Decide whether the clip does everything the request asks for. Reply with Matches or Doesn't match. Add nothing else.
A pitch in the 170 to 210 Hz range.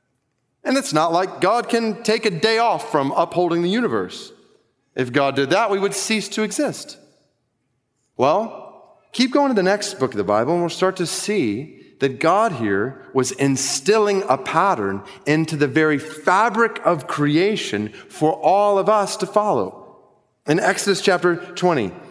Matches